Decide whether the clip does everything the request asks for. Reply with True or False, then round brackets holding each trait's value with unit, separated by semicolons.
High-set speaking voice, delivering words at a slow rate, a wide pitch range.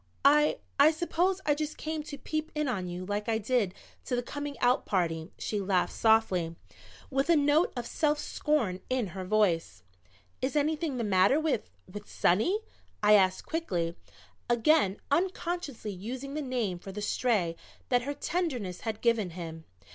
False (240 Hz; 165 wpm; 7.7 semitones)